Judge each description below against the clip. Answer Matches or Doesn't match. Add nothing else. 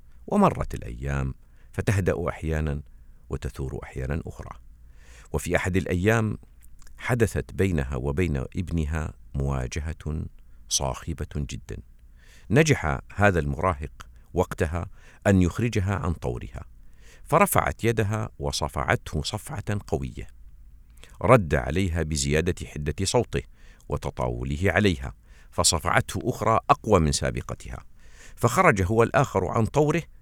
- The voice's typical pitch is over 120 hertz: Doesn't match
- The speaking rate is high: Doesn't match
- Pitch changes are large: Matches